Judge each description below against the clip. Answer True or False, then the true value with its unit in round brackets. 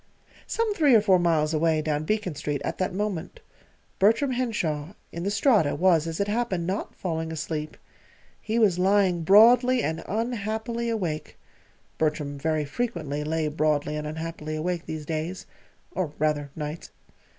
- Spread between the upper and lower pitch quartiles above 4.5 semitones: True (5.5 semitones)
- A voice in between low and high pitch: True (170 Hz)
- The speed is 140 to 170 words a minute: True (150 wpm)